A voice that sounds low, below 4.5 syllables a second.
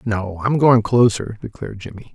No: low, 110 Hz; 5.0 syllables/s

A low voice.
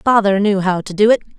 No: high, 200 Hz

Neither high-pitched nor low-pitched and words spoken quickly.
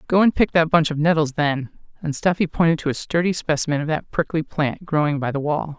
Yes: medium, 155 Hz; fast, 240 wpm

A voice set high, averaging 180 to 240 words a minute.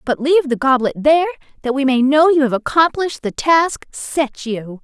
Yes: very high, 280 Hz; average, 200 wpm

